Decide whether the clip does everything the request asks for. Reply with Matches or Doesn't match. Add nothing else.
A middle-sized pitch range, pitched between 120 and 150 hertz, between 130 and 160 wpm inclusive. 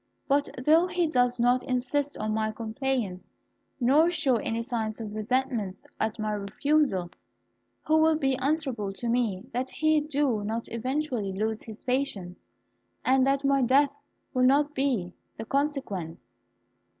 Doesn't match